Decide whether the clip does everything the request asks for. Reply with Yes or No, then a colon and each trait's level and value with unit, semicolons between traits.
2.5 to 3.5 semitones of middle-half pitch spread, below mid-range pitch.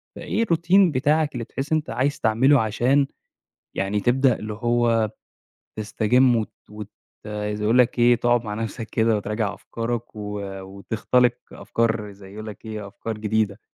Yes: average, 2.9 semitones; low, 115 Hz